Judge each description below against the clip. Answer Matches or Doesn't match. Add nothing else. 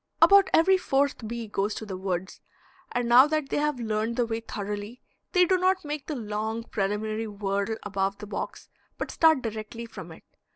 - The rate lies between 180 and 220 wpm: Matches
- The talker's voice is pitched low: Doesn't match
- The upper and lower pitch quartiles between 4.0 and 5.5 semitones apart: Matches